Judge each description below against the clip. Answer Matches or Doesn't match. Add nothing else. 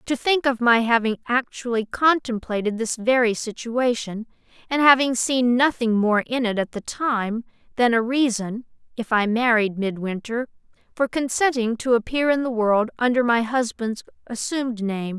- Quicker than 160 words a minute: Doesn't match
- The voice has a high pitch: Matches